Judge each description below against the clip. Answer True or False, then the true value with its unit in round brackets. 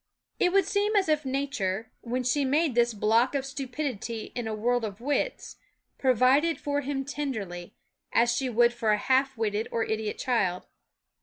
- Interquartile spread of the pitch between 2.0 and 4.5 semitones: True (4.2 semitones)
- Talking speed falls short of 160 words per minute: False (170 wpm)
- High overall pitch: True (250 Hz)